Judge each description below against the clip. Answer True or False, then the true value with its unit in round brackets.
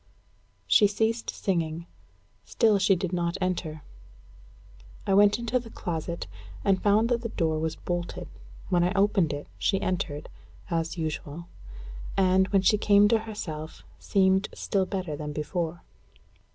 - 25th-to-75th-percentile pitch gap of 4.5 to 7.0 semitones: False (3.7 semitones)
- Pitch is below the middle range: False (185 Hz)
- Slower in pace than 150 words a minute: True (140 wpm)